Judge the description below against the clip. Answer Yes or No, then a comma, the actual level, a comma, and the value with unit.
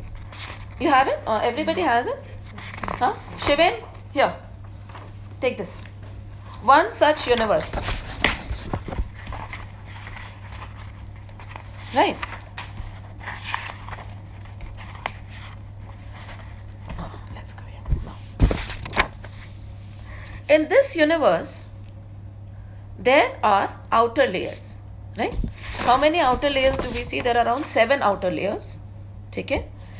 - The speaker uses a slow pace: Yes, slow, 85 wpm